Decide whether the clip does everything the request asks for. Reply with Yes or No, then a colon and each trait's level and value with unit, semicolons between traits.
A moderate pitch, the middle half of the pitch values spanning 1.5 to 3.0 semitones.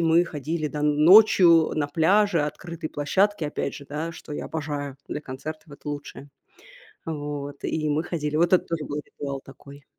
Yes: medium, 150 Hz; narrow, 2.4 semitones